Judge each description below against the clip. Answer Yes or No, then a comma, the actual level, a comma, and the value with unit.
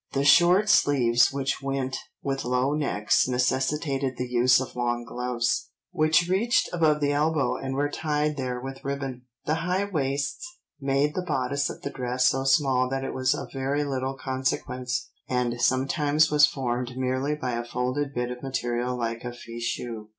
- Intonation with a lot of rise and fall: No, narrow, 2.6 semitones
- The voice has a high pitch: No, low, 135 Hz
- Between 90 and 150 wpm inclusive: No, average, 170 wpm